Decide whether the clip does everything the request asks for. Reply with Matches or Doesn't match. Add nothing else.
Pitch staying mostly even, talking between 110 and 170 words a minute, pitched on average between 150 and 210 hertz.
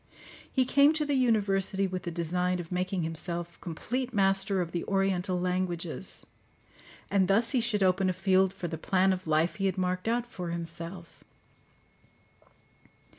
Matches